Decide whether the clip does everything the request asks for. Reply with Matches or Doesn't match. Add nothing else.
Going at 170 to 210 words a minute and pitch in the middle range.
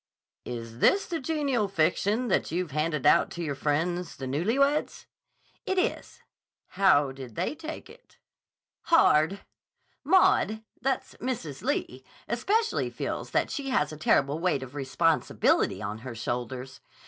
Doesn't match